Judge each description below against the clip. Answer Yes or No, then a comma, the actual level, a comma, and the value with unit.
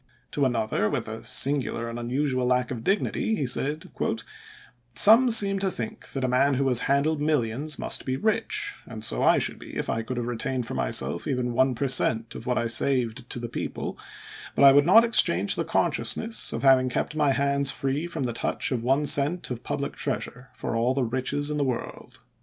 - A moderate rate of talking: No, fast, 210 wpm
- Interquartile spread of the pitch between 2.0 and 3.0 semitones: No, average, 3.4 semitones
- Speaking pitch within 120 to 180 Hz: Yes, low, 135 Hz